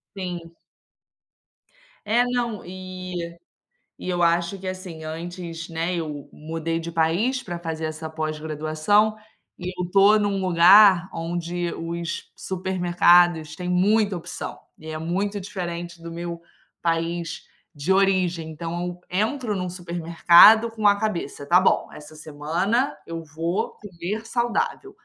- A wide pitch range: No, average, 2.7 semitones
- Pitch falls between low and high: Yes, medium, 175 Hz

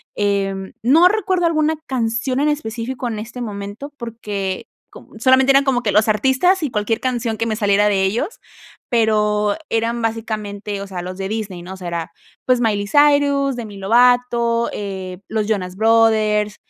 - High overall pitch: Yes, high, 225 Hz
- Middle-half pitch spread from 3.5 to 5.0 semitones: Yes, average, 3.8 semitones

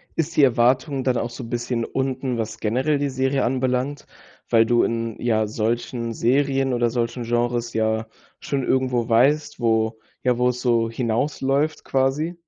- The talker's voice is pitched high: No, low, 125 Hz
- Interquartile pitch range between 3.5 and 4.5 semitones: No, narrow, 2.4 semitones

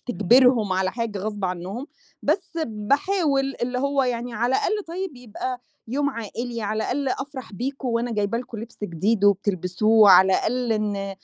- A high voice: Yes, high, 235 Hz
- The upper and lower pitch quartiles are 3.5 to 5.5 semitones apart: Yes, average, 4.3 semitones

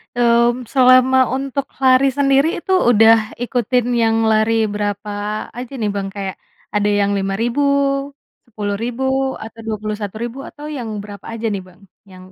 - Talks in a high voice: Yes, high, 230 Hz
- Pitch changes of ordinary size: Yes, average, 3.6 semitones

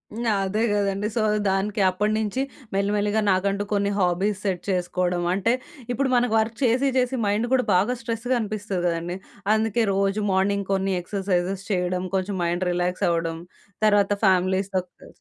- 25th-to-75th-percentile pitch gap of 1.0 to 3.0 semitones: Yes, average, 2.7 semitones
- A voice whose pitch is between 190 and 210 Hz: Yes, high, 200 Hz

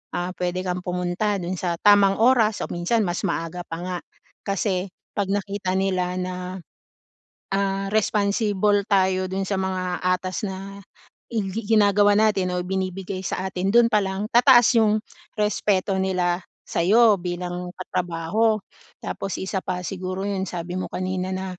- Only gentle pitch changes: Yes, narrow, 2.0 semitones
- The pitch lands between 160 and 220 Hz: Yes, high, 190 Hz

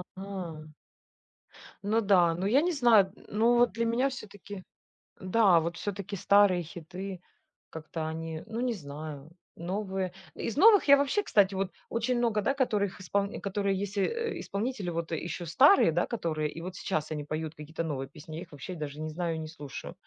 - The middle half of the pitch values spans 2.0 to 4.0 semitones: No, average, 4.9 semitones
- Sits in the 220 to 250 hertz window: No, high, 190 Hz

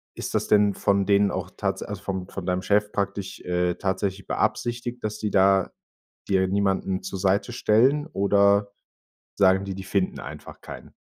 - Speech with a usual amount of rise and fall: No, narrow, 1.4 semitones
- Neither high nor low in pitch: No, low, 100 Hz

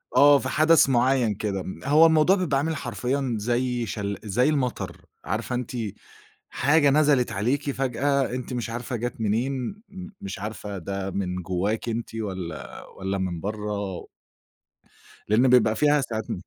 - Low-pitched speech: Yes, low, 120 Hz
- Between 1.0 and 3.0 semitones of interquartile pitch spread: No, average, 5.2 semitones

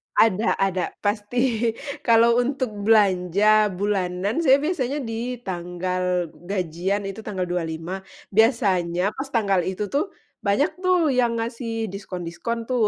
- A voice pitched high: Yes, high, 210 Hz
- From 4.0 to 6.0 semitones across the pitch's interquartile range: Yes, average, 4.3 semitones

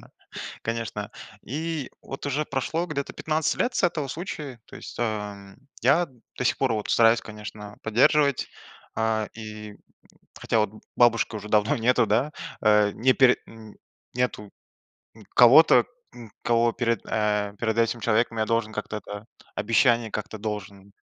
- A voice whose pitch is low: Yes, low, 115 Hz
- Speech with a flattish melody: No, average, 3.1 semitones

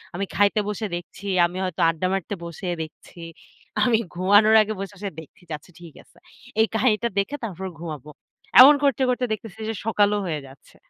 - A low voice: No, high, 200 Hz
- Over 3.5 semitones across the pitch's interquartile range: Yes, average, 4.0 semitones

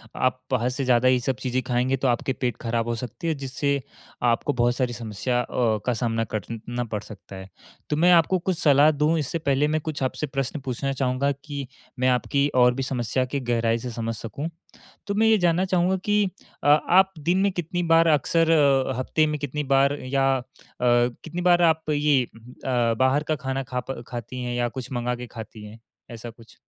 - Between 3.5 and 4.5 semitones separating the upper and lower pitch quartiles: Yes, average, 3.8 semitones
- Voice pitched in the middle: No, low, 130 Hz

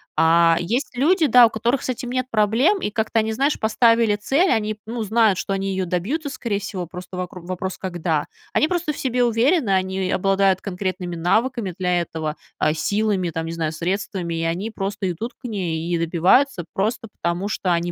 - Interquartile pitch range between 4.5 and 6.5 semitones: Yes, average, 4.8 semitones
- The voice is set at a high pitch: Yes, high, 195 Hz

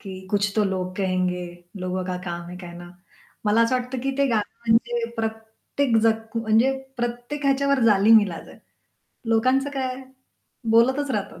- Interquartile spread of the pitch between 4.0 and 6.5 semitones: Yes, average, 4.9 semitones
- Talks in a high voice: Yes, high, 225 Hz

